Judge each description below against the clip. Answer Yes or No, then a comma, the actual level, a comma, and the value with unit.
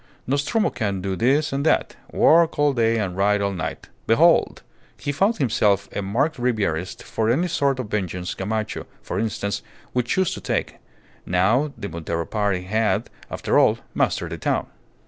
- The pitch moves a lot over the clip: Yes, wide, 5.9 semitones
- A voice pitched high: No, low, 110 Hz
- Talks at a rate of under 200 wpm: Yes, average, 165 wpm